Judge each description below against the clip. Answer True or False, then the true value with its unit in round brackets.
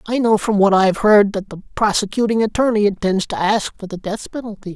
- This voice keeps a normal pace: False (225 wpm)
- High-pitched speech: True (205 Hz)